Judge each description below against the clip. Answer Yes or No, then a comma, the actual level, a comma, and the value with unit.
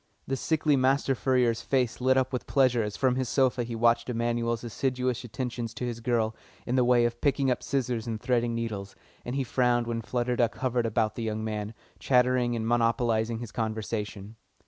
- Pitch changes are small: Yes, narrow, 1.9 semitones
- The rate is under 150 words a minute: No, average, 190 wpm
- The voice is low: Yes, low, 120 Hz